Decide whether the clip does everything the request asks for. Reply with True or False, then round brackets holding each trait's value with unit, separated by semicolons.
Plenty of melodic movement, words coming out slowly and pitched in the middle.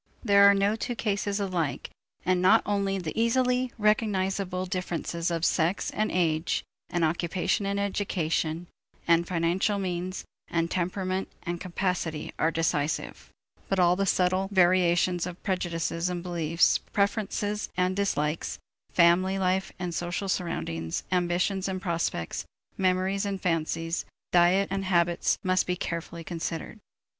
False (2.5 semitones; 130 wpm; 180 Hz)